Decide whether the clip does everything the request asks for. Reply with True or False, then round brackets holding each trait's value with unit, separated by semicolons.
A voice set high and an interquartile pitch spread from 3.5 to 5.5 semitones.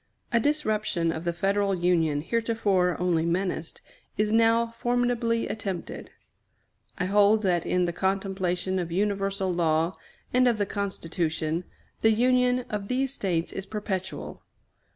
True (195 Hz; 4.1 semitones)